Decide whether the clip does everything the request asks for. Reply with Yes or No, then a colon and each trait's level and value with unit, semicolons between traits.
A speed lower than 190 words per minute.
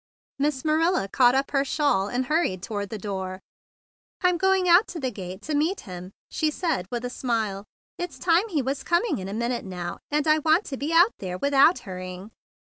No: fast, 205 wpm